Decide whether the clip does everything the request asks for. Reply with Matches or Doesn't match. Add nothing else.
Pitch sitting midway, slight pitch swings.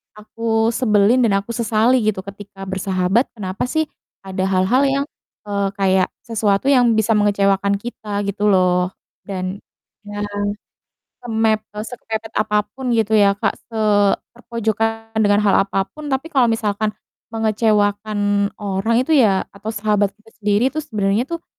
Doesn't match